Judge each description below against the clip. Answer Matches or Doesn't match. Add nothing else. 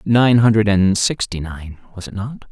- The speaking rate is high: Matches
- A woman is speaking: Doesn't match